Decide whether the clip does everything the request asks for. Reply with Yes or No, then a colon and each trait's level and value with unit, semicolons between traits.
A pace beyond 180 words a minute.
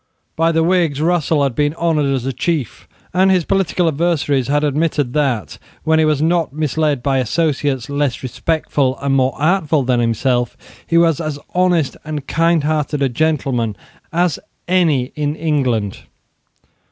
No: average, 155 wpm